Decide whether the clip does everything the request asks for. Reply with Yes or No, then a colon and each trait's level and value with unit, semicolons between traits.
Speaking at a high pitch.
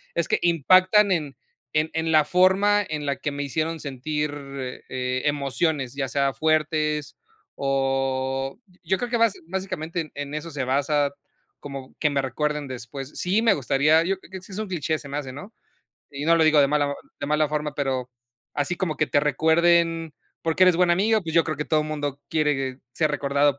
No: medium, 150 Hz